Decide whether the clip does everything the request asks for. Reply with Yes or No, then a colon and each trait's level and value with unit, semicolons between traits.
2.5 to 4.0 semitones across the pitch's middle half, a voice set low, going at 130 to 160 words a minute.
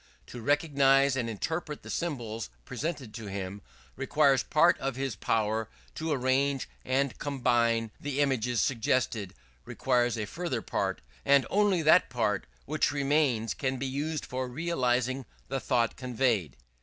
Yes: average, 3.7 semitones; low, 130 Hz; average, 140 wpm